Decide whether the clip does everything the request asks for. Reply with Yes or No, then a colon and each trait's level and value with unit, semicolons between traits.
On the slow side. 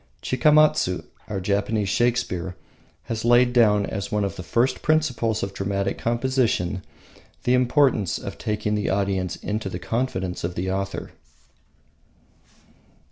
Yes: slow, 130 wpm